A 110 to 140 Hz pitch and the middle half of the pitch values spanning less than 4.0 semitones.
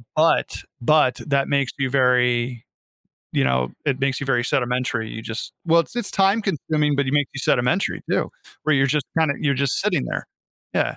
Yes: low, 135 Hz; average, 3.5 semitones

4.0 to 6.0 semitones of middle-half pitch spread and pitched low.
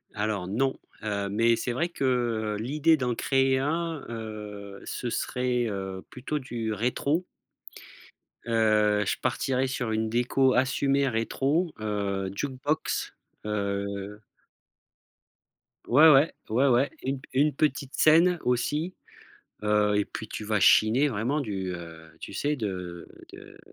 Yes: average, 4.6 semitones; low, 120 Hz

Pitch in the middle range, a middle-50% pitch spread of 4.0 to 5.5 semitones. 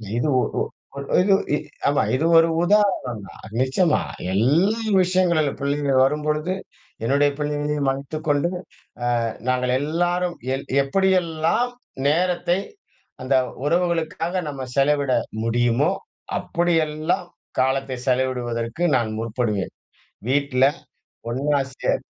Yes: medium, 145 Hz; average, 4.7 semitones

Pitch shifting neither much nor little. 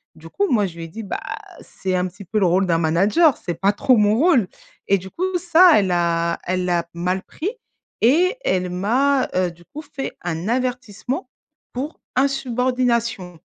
No: wide, 6.6 semitones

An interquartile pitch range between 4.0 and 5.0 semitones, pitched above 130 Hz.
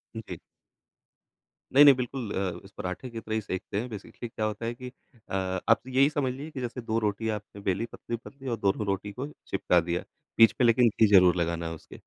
No: average, 4.4 semitones; low, 110 Hz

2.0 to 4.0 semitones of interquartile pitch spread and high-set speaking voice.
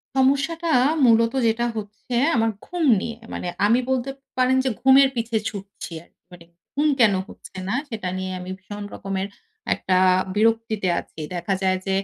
No: average, 4.7 semitones; high, 225 Hz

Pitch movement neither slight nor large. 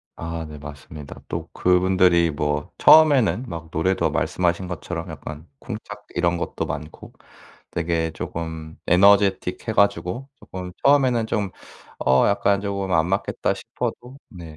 Yes: average, 3.8 semitones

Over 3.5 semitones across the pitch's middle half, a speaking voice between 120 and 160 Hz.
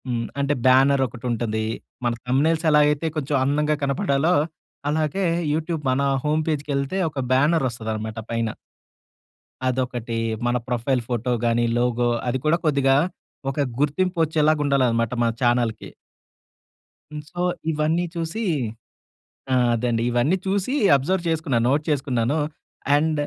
Yes: average, 4.1 semitones; medium, 140 Hz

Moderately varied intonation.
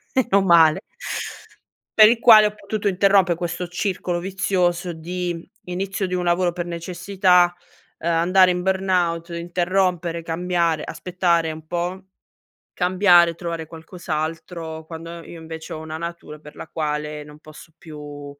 No: narrow, 2.0 semitones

